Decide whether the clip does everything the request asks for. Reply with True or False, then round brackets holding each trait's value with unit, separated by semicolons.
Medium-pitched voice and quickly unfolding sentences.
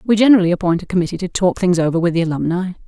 True (180 Hz; 250 wpm)